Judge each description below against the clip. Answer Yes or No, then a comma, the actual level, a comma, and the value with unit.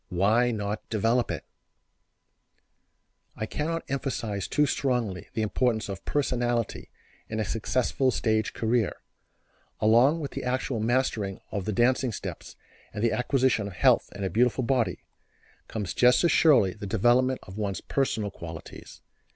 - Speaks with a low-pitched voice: Yes, low, 115 Hz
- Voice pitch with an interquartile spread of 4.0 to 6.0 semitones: No, average, 3.6 semitones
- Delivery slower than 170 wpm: Yes, average, 145 wpm